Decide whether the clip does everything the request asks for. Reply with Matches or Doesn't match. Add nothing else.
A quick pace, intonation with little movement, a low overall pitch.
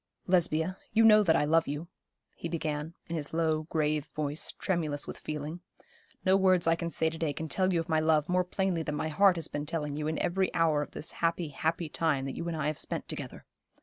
Doesn't match